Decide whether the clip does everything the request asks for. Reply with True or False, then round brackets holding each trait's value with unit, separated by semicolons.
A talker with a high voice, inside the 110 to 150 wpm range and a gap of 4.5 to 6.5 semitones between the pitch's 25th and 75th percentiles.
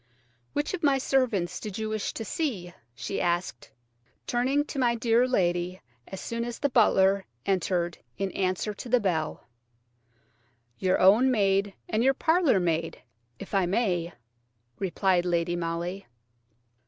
True (195 Hz; 140 wpm; 5.3 semitones)